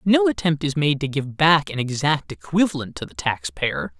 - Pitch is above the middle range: No, medium, 145 Hz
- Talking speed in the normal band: No, fast, 210 wpm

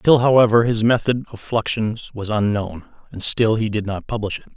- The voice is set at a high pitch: No, low, 110 Hz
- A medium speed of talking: Yes, average, 195 wpm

